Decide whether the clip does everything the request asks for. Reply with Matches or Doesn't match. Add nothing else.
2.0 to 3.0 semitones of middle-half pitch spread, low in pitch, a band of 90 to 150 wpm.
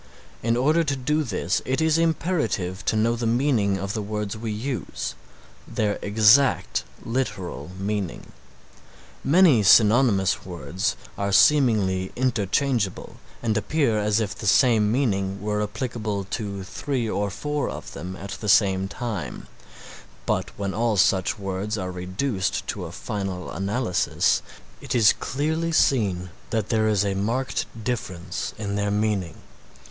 Doesn't match